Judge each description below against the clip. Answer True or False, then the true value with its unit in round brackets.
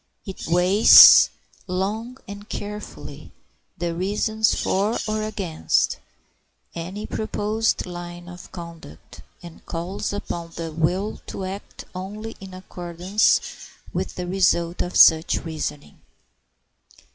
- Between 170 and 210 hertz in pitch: True (185 Hz)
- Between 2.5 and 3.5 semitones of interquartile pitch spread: True (3.1 semitones)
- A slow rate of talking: True (110 wpm)